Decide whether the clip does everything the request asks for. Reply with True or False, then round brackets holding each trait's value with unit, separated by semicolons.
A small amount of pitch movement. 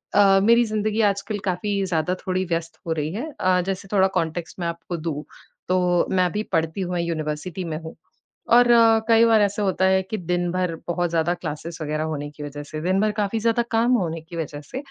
False (3.9 semitones)